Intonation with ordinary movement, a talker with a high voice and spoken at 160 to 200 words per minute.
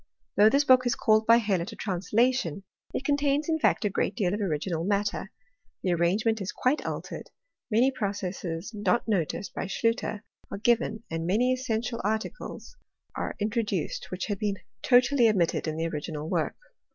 Yes: average, 4.5 semitones; high, 210 Hz; average, 170 wpm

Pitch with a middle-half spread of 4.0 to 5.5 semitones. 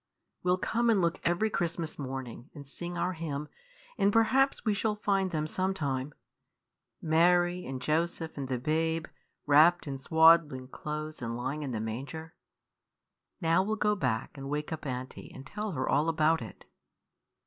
Yes: average, 4.4 semitones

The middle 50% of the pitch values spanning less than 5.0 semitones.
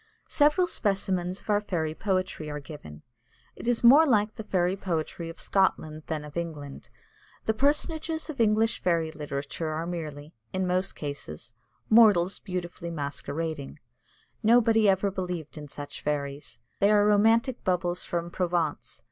No: average, 5.3 semitones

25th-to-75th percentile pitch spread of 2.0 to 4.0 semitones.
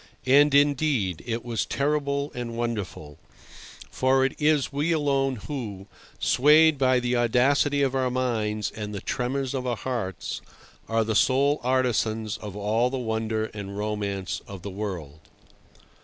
No: average, 4.4 semitones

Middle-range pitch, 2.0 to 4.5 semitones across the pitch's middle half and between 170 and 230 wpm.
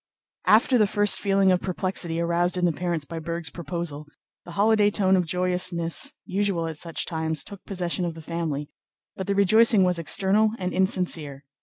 Yes: medium, 180 Hz; average, 2.8 semitones; average, 175 wpm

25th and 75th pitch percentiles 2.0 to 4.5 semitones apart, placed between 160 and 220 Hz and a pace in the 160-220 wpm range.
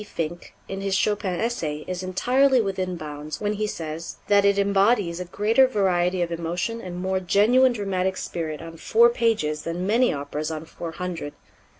Yes: average, 3.9 semitones; medium, 185 Hz; average, 175 wpm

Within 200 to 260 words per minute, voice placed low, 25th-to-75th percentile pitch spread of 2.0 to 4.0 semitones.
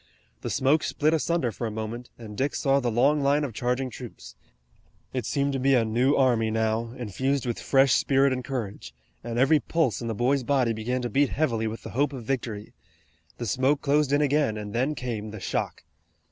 Yes: fast, 205 wpm; low, 125 Hz; average, 3.5 semitones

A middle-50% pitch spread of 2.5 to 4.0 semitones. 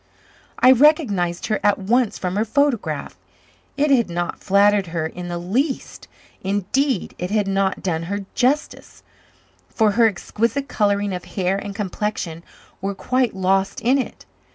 No: average, 4.6 semitones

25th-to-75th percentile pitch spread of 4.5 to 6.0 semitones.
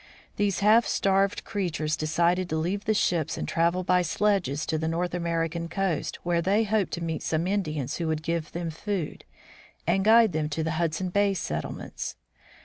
No: average, 3.5 semitones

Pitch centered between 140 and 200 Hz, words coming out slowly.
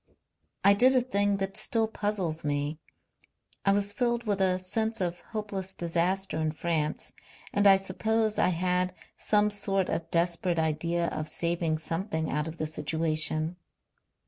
No: medium, 185 Hz; average, 150 wpm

